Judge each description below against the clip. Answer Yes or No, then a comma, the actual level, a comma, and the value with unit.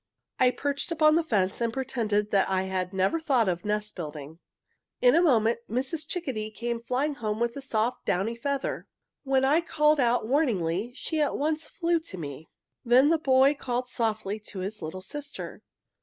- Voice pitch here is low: No, high, 240 Hz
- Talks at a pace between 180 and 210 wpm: Yes, average, 185 wpm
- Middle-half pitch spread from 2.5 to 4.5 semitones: No, wide, 5.6 semitones